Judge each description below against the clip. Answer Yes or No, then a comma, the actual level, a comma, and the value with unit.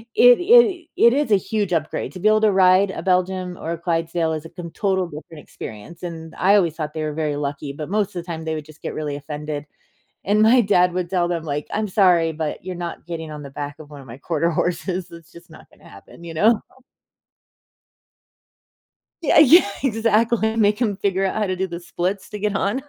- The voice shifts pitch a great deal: No, average, 4.3 semitones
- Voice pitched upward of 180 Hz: No, medium, 175 Hz